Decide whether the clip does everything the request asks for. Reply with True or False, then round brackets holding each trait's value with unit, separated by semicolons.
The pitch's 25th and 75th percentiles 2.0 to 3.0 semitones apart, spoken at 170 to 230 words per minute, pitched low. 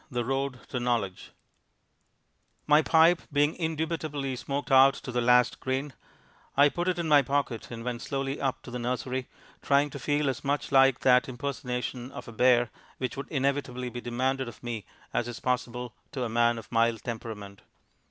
True (2.5 semitones; 180 wpm; 130 Hz)